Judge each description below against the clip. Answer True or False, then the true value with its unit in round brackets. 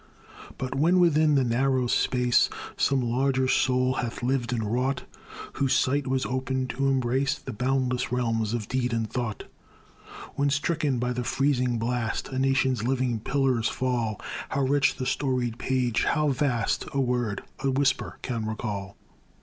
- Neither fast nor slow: True (155 wpm)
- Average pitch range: False (2.1 semitones)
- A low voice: True (130 Hz)